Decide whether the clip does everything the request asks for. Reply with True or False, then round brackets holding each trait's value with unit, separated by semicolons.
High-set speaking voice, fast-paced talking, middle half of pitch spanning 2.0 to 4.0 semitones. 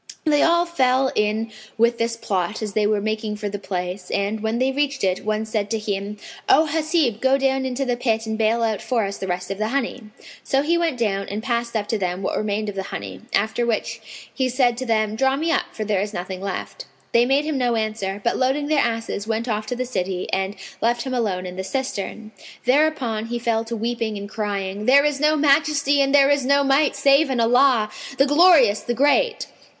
False (230 Hz; 225 wpm; 4.4 semitones)